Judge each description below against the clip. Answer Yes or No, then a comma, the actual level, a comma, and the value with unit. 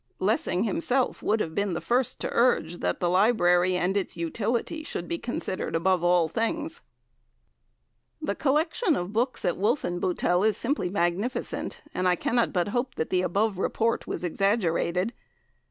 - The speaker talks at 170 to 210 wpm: No, average, 155 wpm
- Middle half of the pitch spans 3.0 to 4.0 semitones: No, average, 5.3 semitones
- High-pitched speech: Yes, high, 200 Hz